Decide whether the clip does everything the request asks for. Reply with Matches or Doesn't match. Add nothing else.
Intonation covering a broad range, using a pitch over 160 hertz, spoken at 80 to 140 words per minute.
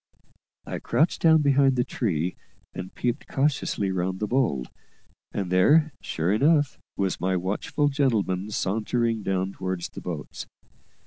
Doesn't match